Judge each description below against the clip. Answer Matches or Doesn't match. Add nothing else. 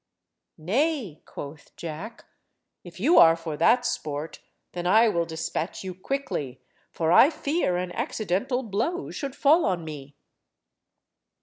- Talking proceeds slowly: Matches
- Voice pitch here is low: Doesn't match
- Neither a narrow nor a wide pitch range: Doesn't match